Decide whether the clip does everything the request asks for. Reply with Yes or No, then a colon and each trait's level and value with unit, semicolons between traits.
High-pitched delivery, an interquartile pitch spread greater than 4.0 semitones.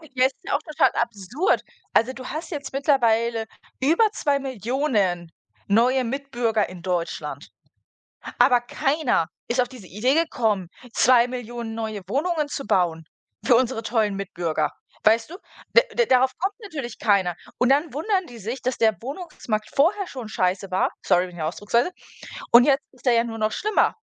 Yes: high, 240 Hz; average, 4.6 semitones